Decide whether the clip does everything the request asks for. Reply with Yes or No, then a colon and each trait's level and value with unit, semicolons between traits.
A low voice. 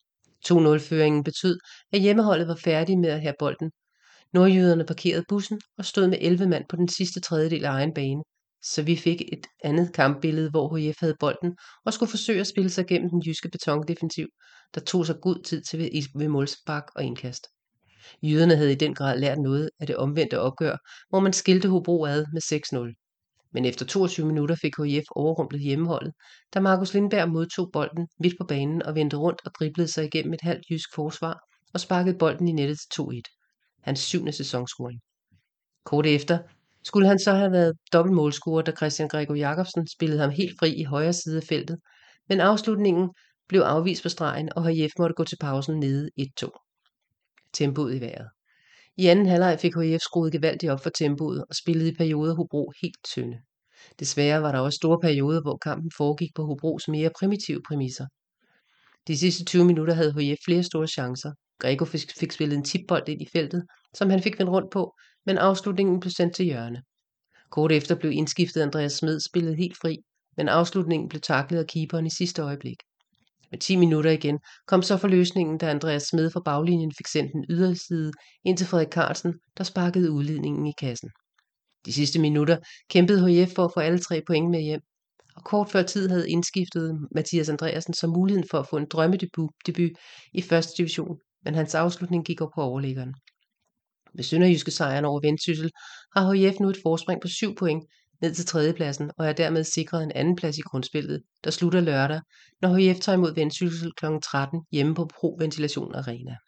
No: medium, 165 Hz